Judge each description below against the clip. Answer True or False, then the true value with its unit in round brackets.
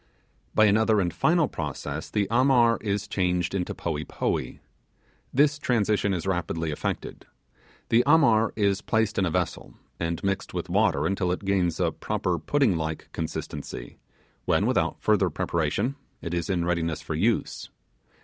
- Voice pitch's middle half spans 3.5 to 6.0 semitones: True (4.9 semitones)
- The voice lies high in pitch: False (95 Hz)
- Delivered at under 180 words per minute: True (150 wpm)